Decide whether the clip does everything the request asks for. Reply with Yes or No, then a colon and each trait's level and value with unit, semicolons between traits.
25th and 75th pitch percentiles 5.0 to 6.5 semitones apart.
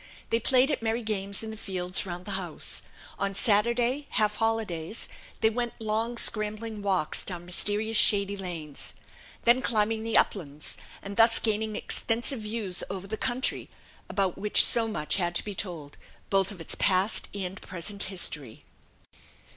No: average, 3.2 semitones